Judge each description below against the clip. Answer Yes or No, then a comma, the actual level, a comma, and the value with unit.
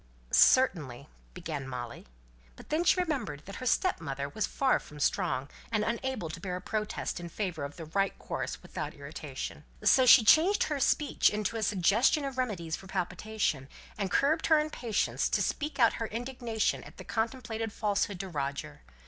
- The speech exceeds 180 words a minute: No, average, 175 wpm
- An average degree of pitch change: No, wide, 7.4 semitones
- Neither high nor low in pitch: No, high, 215 Hz